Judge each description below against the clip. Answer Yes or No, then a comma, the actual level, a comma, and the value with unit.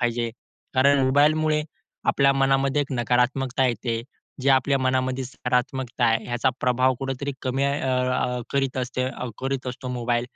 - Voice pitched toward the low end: Yes, low, 130 Hz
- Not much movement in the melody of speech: Yes, narrow, 1.6 semitones